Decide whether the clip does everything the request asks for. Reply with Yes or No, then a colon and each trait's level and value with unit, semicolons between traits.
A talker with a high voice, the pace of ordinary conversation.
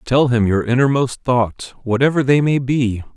No: low, 125 Hz; average, 170 wpm